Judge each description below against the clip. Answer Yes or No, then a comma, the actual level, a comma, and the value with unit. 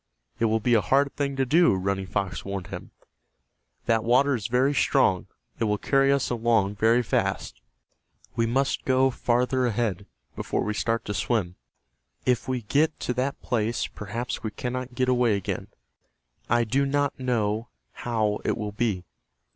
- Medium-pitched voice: No, low, 120 Hz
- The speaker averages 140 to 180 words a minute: Yes, average, 165 wpm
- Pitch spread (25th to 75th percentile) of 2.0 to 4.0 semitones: Yes, average, 3.5 semitones